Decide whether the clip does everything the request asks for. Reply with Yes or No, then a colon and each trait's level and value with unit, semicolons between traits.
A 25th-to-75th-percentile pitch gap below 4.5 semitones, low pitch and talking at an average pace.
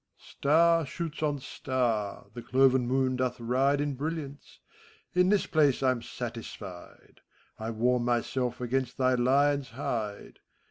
No: average, 2.9 semitones; low, 130 Hz; slow, 130 wpm